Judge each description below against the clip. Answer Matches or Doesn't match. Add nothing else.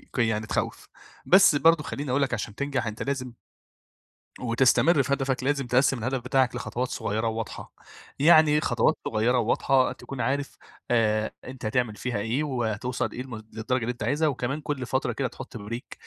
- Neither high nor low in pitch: Doesn't match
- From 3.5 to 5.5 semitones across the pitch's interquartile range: Doesn't match